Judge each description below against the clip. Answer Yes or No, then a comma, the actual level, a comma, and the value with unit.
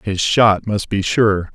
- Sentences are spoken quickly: No, average, 195 wpm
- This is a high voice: No, low, 100 Hz